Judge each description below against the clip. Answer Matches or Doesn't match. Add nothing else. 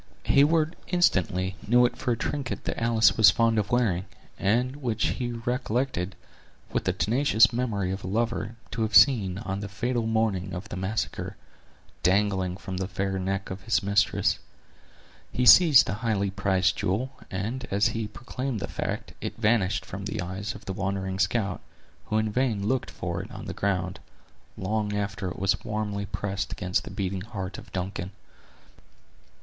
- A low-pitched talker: Matches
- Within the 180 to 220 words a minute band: Doesn't match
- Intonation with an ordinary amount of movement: Matches